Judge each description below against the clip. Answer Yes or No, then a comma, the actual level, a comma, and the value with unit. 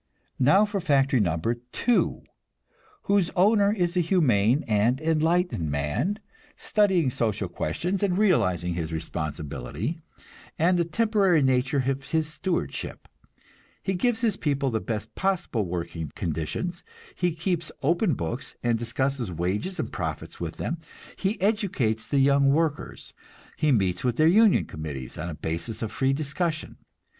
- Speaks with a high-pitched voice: No, medium, 140 Hz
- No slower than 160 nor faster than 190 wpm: No, average, 140 wpm